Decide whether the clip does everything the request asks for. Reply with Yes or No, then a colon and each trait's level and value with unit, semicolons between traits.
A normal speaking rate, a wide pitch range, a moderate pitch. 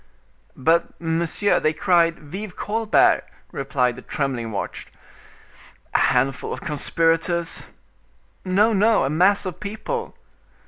No: slow, 110 wpm; wide, 5.7 semitones; medium, 165 Hz